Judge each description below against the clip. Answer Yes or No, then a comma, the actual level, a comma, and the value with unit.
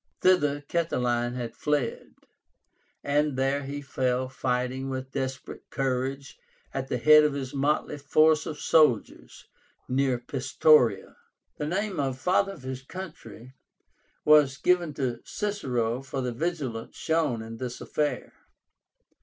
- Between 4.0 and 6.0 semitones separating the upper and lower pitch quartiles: No, average, 3.0 semitones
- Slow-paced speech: Yes, slow, 130 wpm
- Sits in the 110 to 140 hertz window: Yes, low, 135 Hz